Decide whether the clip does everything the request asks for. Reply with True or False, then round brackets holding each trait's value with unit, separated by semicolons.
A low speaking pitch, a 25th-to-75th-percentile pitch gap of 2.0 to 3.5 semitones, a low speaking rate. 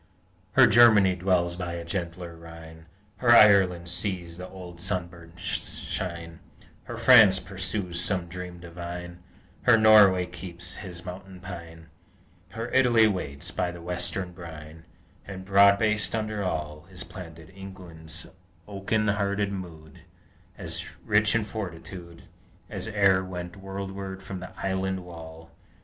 True (90 Hz; 2.4 semitones; 130 wpm)